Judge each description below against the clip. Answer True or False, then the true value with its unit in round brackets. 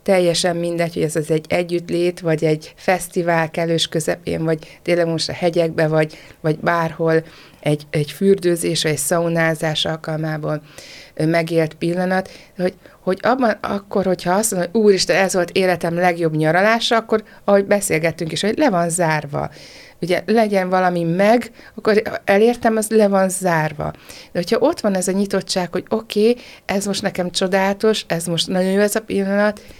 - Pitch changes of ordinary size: True (3.4 semitones)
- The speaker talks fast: True (165 wpm)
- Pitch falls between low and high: True (180 Hz)